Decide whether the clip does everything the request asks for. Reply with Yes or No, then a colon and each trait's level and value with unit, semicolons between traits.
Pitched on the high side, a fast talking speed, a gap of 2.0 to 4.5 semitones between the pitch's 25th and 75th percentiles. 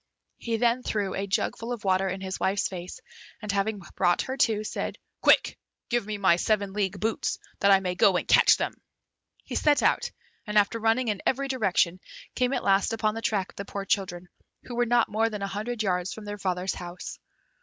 Yes: high, 205 Hz; fast, 210 wpm; average, 2.9 semitones